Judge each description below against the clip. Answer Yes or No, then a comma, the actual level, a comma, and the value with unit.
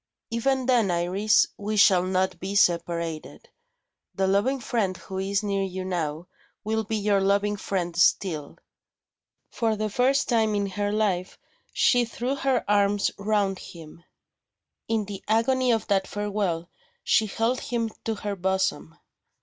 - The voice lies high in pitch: Yes, high, 200 Hz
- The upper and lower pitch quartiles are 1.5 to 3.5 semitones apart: Yes, average, 2.8 semitones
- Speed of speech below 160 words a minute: Yes, average, 145 wpm